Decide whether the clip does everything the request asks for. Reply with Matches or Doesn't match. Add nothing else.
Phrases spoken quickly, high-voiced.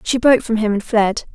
Matches